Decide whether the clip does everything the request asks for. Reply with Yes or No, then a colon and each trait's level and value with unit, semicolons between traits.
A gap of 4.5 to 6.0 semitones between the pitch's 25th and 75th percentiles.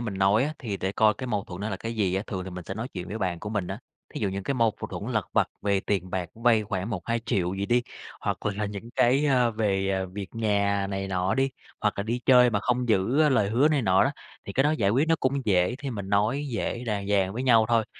No: average, 3.8 semitones